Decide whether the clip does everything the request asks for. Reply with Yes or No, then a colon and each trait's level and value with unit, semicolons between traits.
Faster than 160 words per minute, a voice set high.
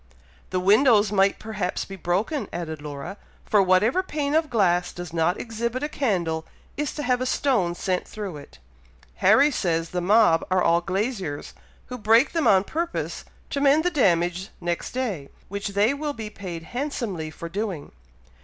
Yes: average, 170 wpm; high, 200 Hz